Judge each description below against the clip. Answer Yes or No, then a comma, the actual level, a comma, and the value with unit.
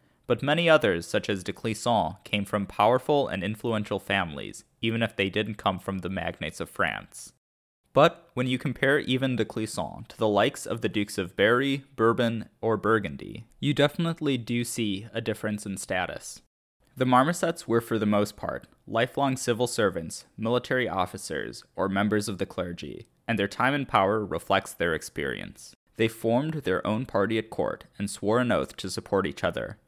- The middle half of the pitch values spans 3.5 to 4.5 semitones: Yes, average, 4.1 semitones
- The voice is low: Yes, low, 110 Hz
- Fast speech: No, average, 180 wpm